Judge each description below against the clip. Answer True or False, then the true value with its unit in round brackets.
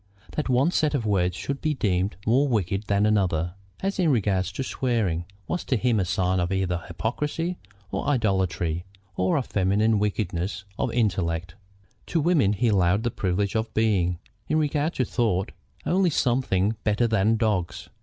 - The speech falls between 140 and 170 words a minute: True (165 wpm)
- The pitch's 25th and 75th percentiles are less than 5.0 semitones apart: False (5.3 semitones)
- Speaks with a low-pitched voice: True (105 Hz)